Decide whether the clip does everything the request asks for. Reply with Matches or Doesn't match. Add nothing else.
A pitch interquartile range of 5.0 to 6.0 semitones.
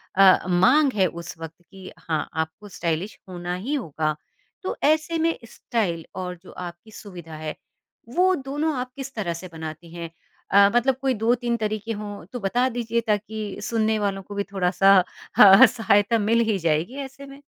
Matches